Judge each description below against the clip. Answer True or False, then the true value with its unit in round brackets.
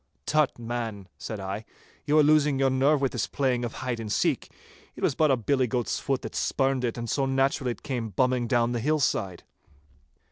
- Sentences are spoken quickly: True (210 wpm)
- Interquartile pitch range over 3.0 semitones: False (2.7 semitones)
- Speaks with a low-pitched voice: True (130 Hz)